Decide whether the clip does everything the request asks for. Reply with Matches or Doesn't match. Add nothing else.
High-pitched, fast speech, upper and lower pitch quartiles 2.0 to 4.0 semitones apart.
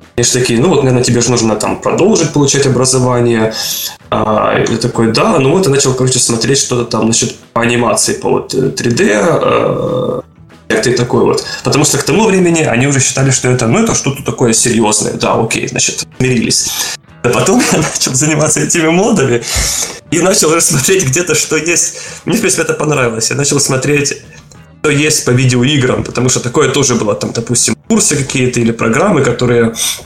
Doesn't match